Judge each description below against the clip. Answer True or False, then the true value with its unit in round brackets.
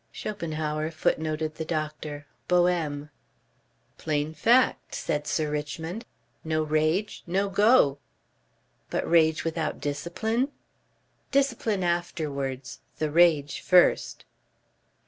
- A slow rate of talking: True (90 wpm)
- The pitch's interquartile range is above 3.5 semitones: False (2.8 semitones)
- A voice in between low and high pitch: True (160 Hz)